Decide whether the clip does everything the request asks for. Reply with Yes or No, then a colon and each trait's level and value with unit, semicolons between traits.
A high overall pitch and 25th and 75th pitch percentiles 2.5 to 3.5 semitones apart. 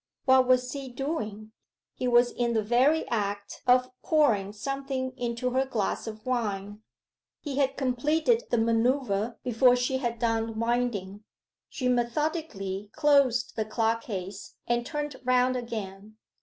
Yes: high, 240 Hz; average, 3.2 semitones